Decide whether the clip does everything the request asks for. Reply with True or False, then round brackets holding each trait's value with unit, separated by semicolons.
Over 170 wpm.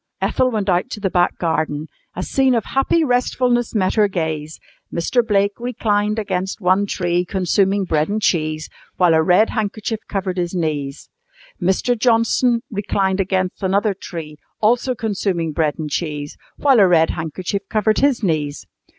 False (160 wpm)